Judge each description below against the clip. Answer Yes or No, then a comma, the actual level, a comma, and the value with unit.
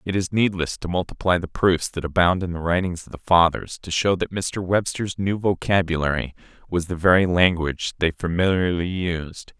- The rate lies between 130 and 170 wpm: No, average, 180 wpm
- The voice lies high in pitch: No, very low, 90 Hz